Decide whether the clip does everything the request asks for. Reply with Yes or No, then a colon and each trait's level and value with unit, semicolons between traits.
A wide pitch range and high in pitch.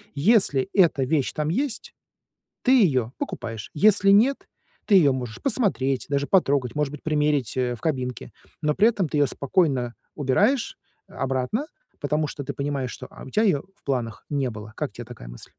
No: wide, 6.6 semitones; medium, 145 Hz